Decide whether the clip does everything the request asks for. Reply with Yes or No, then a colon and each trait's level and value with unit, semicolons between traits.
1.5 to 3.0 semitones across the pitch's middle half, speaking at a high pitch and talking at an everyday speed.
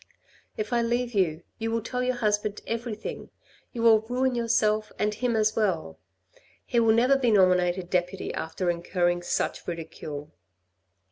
No: average, 4.6 semitones; high, 215 Hz; average, 150 wpm